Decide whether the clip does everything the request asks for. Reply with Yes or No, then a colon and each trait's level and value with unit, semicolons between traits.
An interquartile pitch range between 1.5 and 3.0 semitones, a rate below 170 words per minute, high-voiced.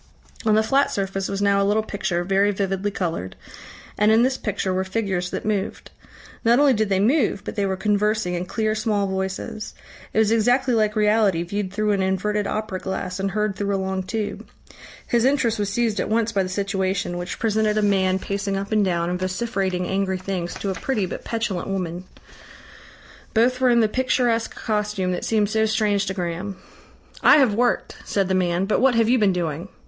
No: narrow, 2.5 semitones; fast, 205 wpm; high, 200 Hz